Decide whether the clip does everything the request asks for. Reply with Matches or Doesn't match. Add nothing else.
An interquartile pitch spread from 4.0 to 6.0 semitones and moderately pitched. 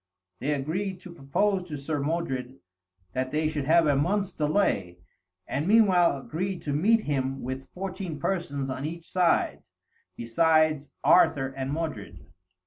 Matches